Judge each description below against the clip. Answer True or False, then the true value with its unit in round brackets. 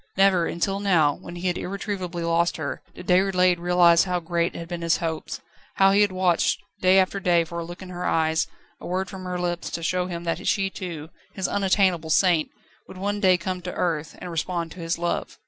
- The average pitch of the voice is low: False (180 Hz)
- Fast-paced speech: True (215 wpm)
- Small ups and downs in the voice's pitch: True (1.8 semitones)